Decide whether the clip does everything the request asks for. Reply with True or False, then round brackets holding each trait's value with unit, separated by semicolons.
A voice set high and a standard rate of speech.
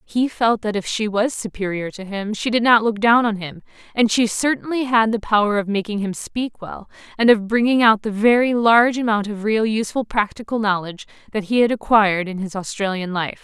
False (215 Hz; 215 wpm)